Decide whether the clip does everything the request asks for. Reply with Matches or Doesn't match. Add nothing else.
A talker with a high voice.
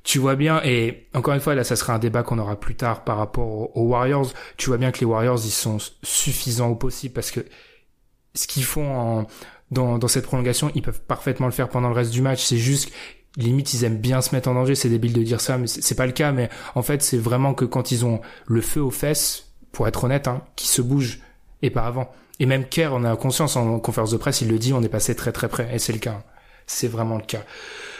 Doesn't match